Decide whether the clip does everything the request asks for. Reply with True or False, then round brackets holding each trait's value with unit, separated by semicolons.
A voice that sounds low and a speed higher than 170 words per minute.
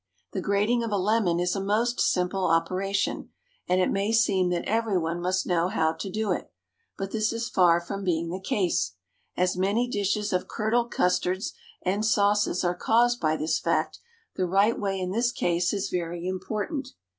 False (195 Hz; 185 wpm)